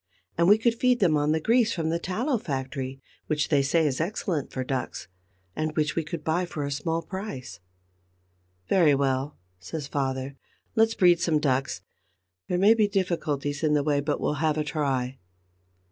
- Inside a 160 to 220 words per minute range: Yes, average, 180 wpm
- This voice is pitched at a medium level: Yes, medium, 155 Hz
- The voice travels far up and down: No, average, 4.2 semitones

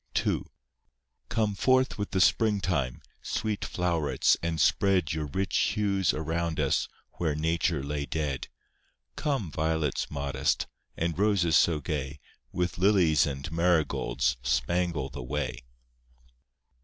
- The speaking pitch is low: Yes, very low, 80 Hz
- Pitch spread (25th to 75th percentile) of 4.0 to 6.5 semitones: Yes, average, 4.4 semitones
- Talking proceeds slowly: Yes, slow, 120 wpm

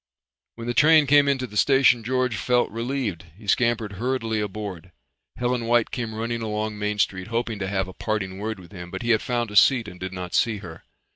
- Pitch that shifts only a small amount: No, average, 3.5 semitones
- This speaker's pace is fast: Yes, fast, 215 wpm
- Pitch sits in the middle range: No, low, 110 Hz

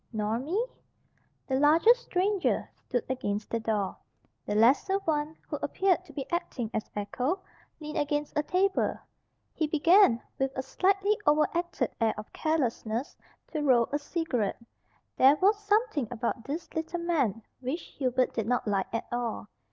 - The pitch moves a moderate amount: No, wide, 6.6 semitones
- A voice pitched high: Yes, very high, 290 Hz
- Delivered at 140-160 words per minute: Yes, average, 150 wpm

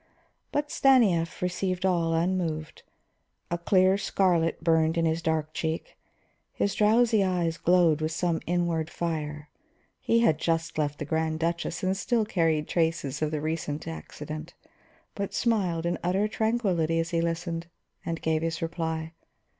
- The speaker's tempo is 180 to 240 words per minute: No, average, 150 wpm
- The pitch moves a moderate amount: No, narrow, 2.3 semitones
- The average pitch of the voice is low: No, medium, 165 Hz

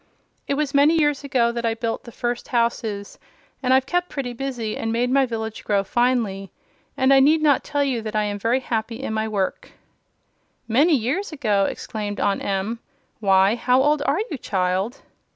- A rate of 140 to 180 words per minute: No, average, 190 wpm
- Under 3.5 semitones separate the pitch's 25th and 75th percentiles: No, average, 4.1 semitones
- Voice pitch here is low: No, high, 235 Hz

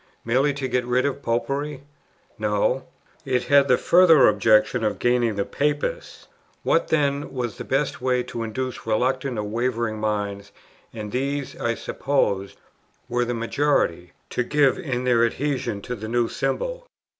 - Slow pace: No, average, 155 wpm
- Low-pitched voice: Yes, low, 125 Hz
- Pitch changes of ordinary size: Yes, average, 3.7 semitones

